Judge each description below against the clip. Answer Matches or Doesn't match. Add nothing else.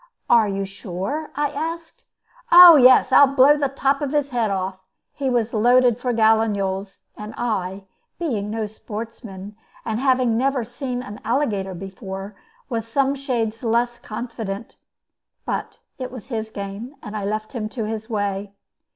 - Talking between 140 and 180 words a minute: Matches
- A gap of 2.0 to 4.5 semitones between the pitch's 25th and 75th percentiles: Matches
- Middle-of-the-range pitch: Doesn't match